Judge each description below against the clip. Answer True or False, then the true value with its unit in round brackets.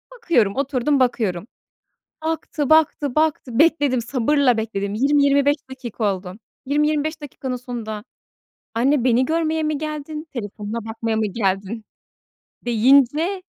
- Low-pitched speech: False (260 Hz)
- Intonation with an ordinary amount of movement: True (4.9 semitones)